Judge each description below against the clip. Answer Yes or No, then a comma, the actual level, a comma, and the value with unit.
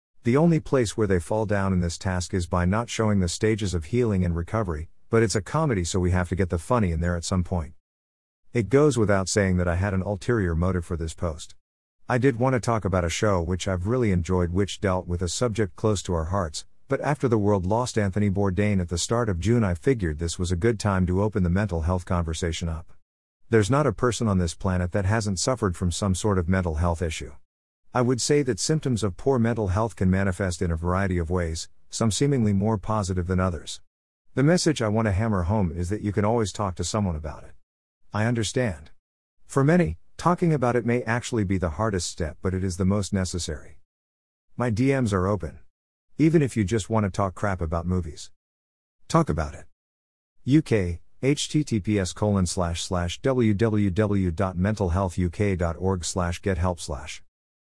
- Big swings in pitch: No, average, 4.2 semitones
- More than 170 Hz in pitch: No, very low, 95 Hz